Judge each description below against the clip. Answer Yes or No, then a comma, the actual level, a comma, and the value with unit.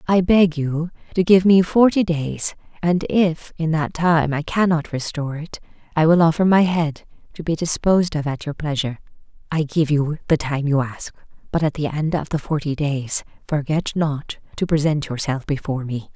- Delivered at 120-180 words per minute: No, average, 190 wpm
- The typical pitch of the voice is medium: Yes, medium, 155 Hz